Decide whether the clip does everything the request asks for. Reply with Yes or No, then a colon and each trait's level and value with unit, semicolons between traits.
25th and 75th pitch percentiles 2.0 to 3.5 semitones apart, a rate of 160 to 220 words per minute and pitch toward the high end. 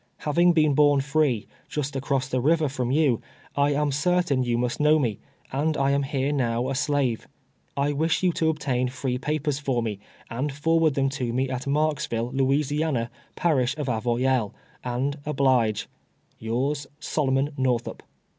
No: average, 3.0 semitones; average, 165 wpm; low, 135 Hz